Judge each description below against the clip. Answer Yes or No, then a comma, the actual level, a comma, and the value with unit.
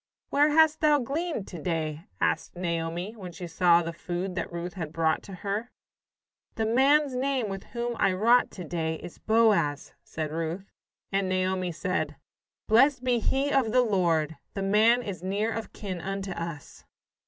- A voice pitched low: No, high, 195 Hz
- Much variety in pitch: Yes, wide, 5.8 semitones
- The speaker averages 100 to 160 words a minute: No, average, 170 wpm